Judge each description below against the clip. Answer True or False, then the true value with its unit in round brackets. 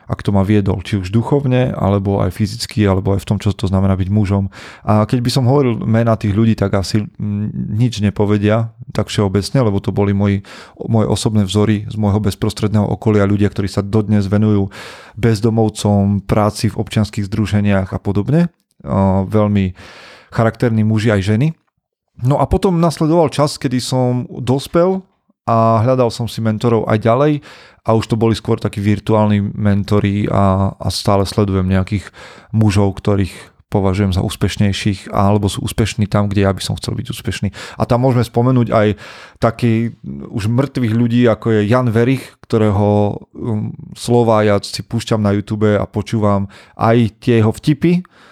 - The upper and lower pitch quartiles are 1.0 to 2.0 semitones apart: False (2.5 semitones)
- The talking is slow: False (160 wpm)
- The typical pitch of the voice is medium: False (105 Hz)